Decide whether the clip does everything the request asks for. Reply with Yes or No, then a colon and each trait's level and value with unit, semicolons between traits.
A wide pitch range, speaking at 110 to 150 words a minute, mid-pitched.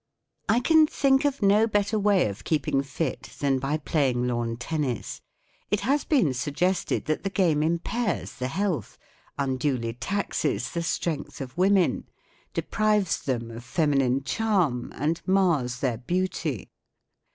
Yes: wide, 7.4 semitones; average, 145 wpm; medium, 155 Hz